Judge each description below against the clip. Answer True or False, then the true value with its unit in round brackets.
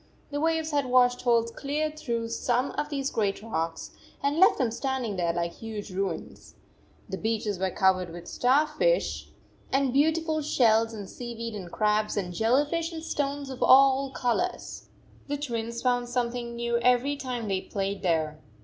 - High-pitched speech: True (240 Hz)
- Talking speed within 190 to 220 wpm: False (170 wpm)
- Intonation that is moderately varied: True (4.9 semitones)